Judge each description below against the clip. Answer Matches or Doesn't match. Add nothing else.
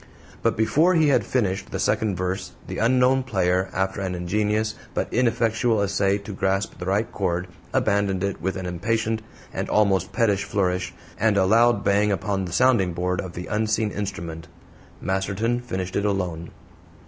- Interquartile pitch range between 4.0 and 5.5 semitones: Doesn't match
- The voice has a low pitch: Matches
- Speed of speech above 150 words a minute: Matches